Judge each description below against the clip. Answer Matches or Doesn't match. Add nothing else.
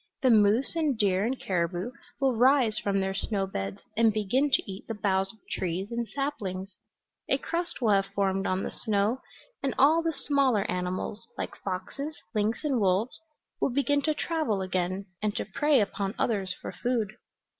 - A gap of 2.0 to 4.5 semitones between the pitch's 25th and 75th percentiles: Doesn't match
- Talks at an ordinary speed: Matches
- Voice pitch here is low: Doesn't match